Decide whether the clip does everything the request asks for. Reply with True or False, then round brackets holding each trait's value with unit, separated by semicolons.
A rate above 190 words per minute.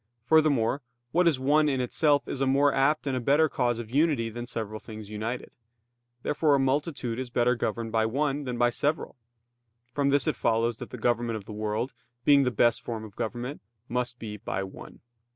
True (200 wpm)